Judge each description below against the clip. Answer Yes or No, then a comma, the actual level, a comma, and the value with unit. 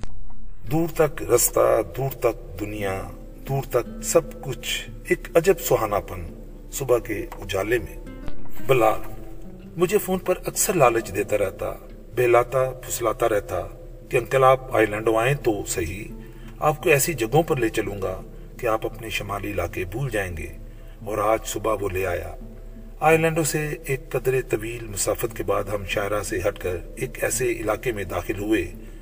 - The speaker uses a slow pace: No, average, 160 wpm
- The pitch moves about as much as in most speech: No, wide, 5.9 semitones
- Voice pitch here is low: Yes, low, 115 Hz